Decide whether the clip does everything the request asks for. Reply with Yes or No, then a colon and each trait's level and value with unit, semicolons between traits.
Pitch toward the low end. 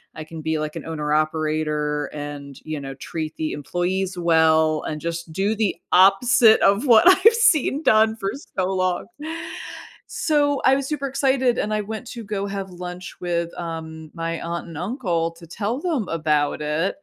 No: medium, 175 Hz